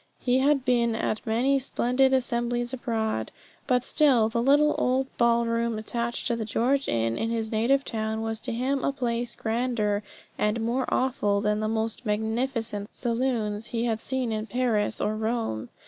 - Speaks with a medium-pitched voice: No, high, 235 Hz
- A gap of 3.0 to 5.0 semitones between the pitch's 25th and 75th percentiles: No, narrow, 2.4 semitones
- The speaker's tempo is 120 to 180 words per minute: Yes, average, 165 wpm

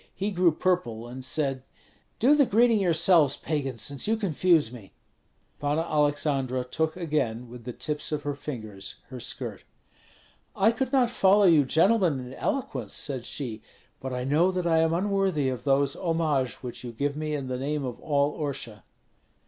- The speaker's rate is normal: Yes, average, 175 wpm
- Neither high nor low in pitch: Yes, medium, 150 Hz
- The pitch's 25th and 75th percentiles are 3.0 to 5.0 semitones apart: No, wide, 5.5 semitones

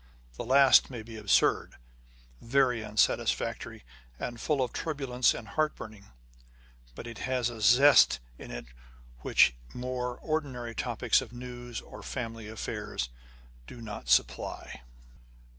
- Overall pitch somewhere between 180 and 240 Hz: No, low, 120 Hz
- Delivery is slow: Yes, slow, 125 wpm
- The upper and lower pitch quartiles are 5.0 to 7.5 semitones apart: No, narrow, 2.6 semitones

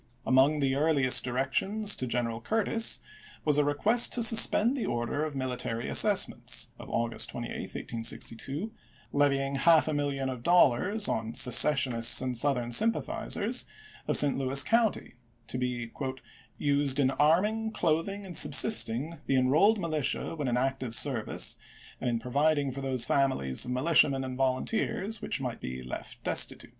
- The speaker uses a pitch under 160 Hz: Yes, medium, 140 Hz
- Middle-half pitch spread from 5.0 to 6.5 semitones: No, average, 4.5 semitones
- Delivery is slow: No, average, 155 wpm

